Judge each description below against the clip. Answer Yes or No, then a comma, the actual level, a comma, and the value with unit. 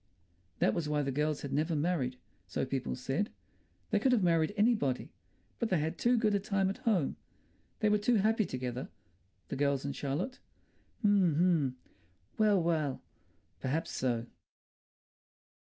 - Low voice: No, medium, 160 Hz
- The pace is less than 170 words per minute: Yes, average, 155 wpm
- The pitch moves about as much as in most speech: No, wide, 6.9 semitones